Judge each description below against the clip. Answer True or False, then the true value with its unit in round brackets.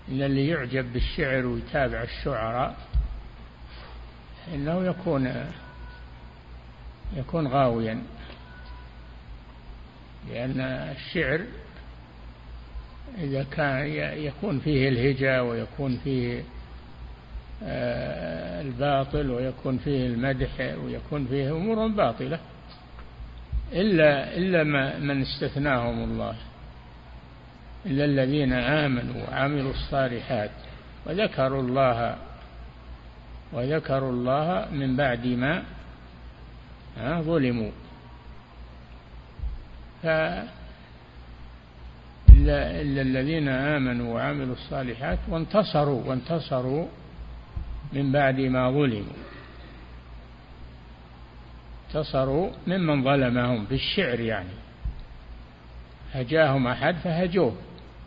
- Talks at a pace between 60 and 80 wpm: True (70 wpm)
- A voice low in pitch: True (125 Hz)